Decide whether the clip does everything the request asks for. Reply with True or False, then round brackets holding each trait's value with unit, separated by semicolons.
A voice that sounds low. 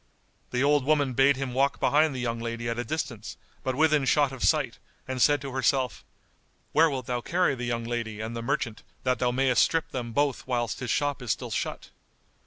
True (130 Hz)